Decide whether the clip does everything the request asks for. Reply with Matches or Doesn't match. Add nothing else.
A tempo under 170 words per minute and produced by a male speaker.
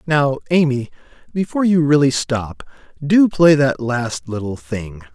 Matches